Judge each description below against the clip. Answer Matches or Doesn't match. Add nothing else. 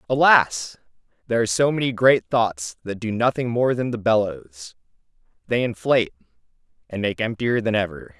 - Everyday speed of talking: Matches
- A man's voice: Matches